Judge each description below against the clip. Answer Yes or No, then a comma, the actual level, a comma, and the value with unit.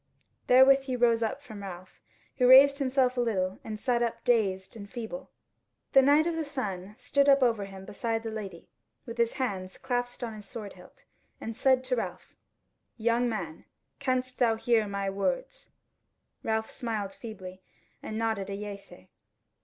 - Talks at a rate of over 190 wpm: No, average, 170 wpm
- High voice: Yes, high, 230 Hz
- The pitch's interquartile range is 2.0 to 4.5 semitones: Yes, average, 4.2 semitones